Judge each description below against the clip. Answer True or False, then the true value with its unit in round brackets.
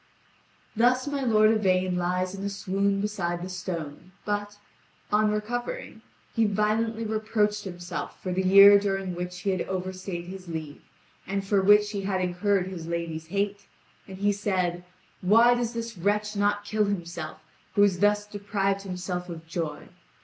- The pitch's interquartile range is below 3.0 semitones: True (2.5 semitones)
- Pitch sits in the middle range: False (195 Hz)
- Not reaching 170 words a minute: True (160 wpm)